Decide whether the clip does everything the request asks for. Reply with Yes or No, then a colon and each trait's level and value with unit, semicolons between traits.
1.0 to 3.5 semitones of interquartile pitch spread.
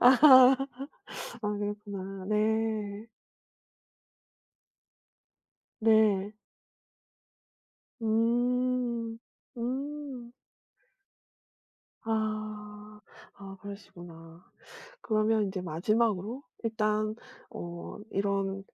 Yes: narrow, 2.5 semitones